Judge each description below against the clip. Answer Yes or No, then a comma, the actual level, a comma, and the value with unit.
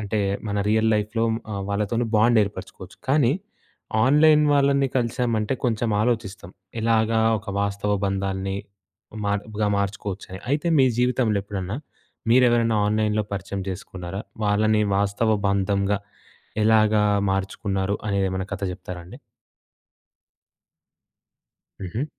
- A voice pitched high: No, low, 105 Hz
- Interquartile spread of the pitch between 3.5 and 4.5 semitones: No, average, 2.7 semitones